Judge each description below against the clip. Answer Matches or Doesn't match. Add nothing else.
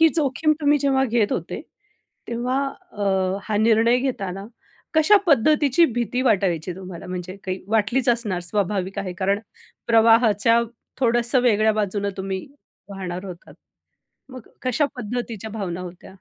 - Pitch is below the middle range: Doesn't match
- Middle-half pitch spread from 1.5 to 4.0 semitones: Doesn't match